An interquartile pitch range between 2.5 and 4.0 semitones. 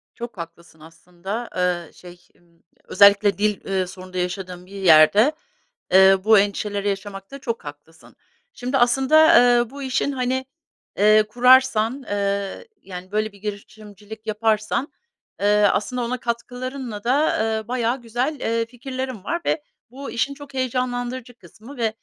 No: average, 4.4 semitones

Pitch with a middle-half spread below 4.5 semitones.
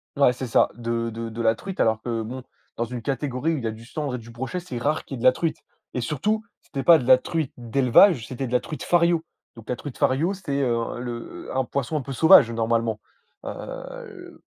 No: average, 5.1 semitones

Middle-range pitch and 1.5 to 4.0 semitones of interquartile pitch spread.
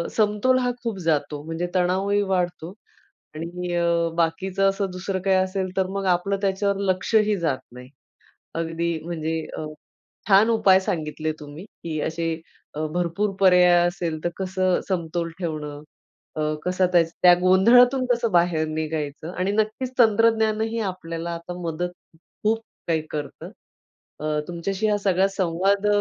Yes: medium, 180 Hz; average, 3.3 semitones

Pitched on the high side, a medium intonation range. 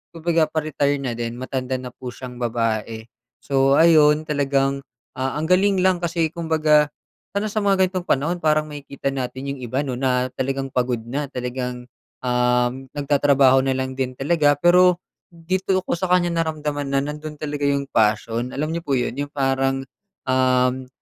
No: medium, 140 Hz; average, 3.4 semitones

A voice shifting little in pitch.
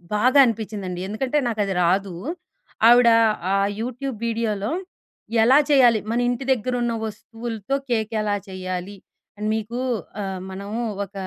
No: average, 3.1 semitones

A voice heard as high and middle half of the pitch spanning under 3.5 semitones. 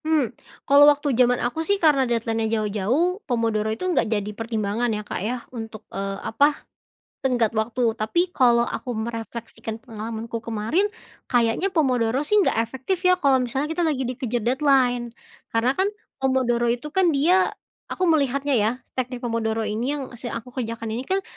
No: high, 245 Hz; average, 3.8 semitones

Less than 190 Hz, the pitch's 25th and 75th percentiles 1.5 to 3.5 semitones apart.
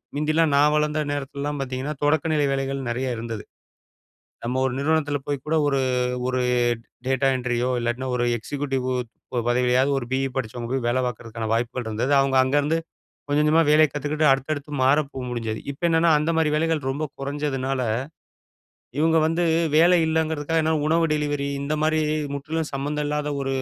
Yes: medium, 140 Hz; average, 2.9 semitones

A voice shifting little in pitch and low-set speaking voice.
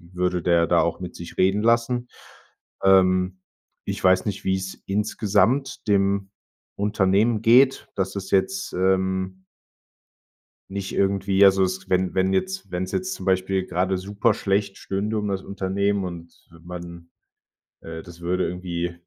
Yes: narrow, 1.7 semitones; very low, 95 Hz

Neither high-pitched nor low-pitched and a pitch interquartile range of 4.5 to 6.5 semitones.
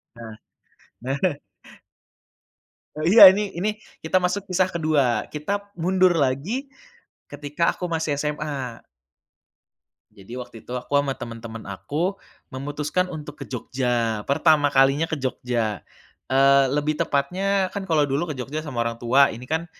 Yes: medium, 145 Hz; average, 5.1 semitones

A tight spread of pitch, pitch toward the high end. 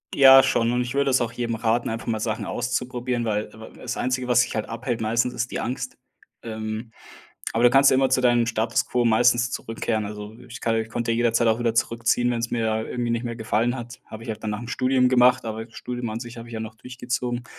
No: narrow, 1.6 semitones; low, 120 Hz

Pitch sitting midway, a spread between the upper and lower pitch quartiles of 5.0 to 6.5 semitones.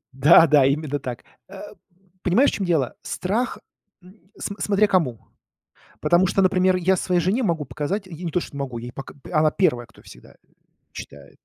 Yes: medium, 175 Hz; average, 5.3 semitones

